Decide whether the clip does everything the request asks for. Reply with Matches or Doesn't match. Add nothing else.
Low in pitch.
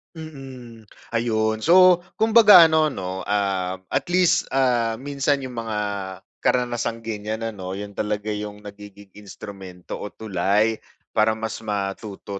Matches